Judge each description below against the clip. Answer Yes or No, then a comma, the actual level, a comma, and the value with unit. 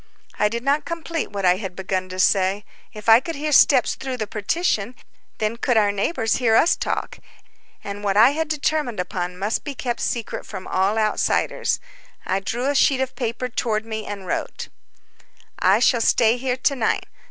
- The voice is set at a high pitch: Yes, high, 225 Hz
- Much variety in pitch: No, average, 4.5 semitones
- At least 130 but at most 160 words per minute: No, average, 185 wpm